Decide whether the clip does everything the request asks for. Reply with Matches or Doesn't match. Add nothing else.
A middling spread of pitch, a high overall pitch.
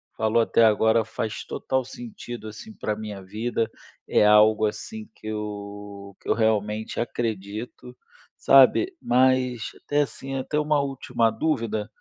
Doesn't match